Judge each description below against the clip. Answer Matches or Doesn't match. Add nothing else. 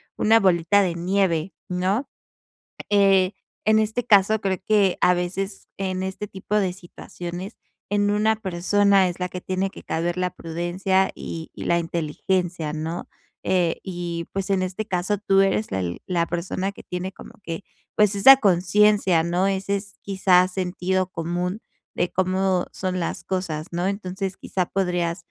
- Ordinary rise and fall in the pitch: Doesn't match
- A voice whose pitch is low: Doesn't match